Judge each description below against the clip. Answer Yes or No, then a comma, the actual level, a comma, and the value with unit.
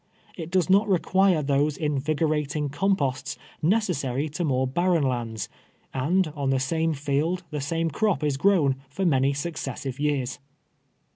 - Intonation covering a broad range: No, average, 4.0 semitones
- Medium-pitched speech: Yes, medium, 150 Hz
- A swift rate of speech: No, average, 145 wpm